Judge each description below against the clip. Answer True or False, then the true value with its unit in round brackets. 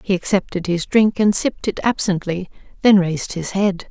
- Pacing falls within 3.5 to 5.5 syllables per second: True (5.2 syllables/s)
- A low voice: False (190 Hz)